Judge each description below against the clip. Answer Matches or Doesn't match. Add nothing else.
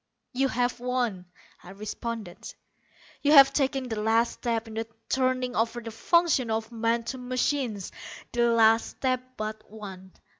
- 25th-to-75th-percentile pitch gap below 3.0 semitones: Matches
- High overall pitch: Matches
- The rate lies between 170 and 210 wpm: Doesn't match